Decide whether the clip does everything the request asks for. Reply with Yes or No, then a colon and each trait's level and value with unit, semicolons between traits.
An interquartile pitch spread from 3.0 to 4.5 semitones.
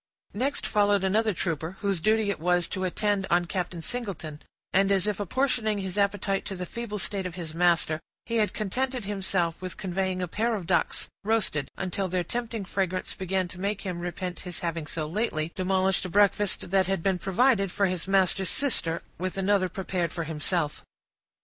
No: narrow, 2.6 semitones